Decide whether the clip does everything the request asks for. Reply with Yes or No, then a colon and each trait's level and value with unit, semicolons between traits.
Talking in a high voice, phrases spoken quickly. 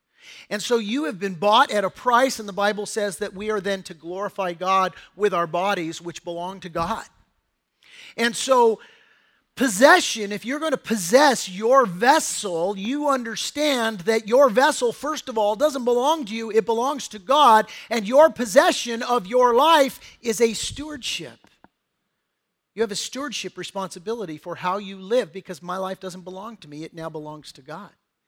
No: high, 220 Hz; average, 175 wpm